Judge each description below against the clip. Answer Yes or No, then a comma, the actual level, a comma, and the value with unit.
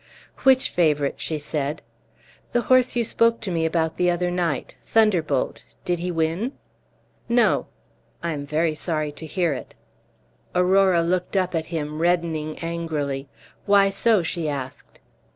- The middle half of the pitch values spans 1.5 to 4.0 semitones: Yes, average, 3.4 semitones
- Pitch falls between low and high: Yes, medium, 170 Hz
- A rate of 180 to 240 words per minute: No, average, 145 wpm